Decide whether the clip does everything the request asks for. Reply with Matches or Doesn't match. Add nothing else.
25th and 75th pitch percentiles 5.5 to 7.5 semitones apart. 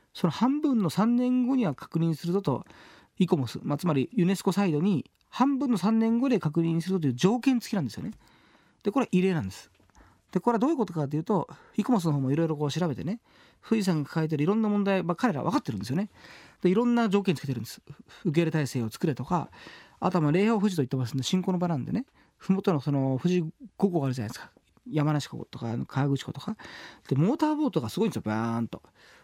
Matches